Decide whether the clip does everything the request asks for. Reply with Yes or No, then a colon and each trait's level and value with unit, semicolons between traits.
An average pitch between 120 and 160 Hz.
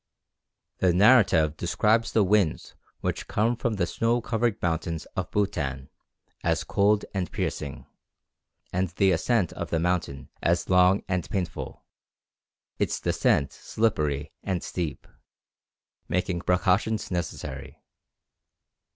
No: very low, 90 Hz